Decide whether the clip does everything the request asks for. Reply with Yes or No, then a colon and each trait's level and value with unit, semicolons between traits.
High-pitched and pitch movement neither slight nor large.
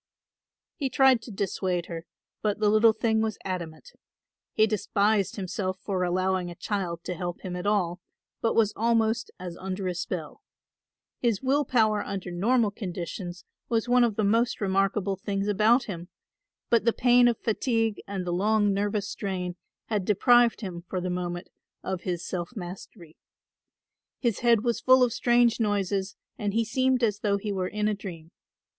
Yes: high, 205 Hz; average, 3.7 semitones